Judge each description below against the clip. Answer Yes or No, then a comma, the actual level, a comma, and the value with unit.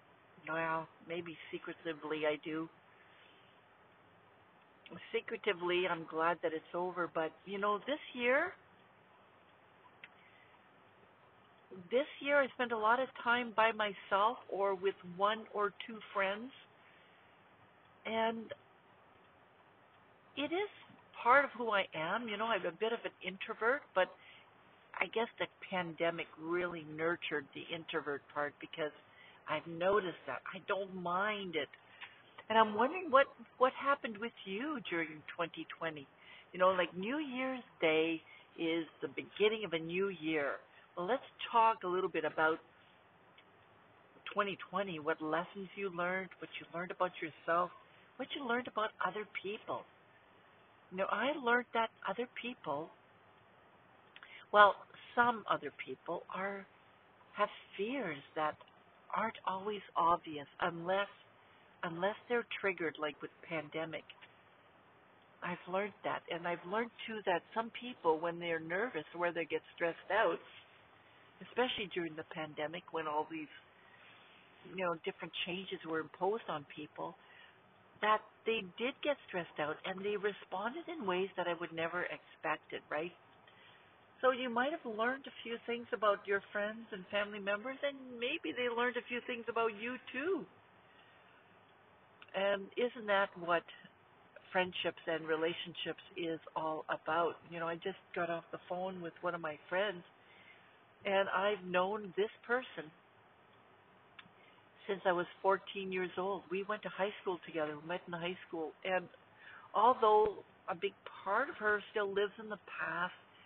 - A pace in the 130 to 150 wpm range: Yes, average, 145 wpm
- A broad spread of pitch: No, average, 4.9 semitones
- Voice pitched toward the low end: No, high, 190 Hz